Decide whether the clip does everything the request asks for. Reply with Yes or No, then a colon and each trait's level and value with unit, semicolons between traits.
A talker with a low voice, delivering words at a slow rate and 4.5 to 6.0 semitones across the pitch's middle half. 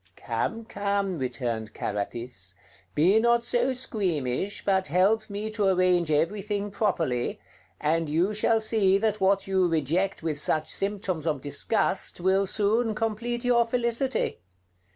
No: high, 195 Hz; slow, 130 wpm; wide, 5.4 semitones